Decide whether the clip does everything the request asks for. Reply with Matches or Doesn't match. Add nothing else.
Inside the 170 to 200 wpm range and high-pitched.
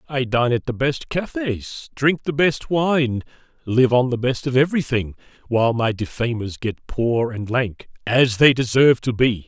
Doesn't match